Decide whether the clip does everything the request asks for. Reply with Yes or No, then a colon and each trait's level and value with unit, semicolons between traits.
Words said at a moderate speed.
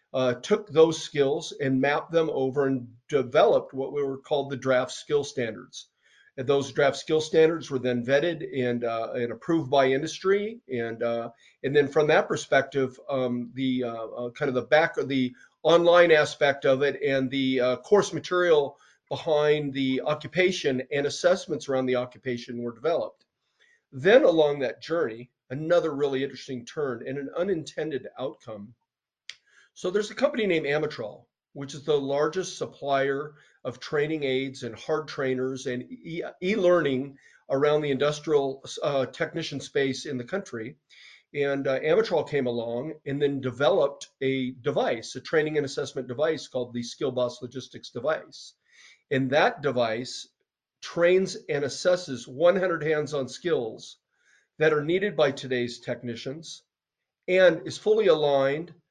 Yes: average, 150 wpm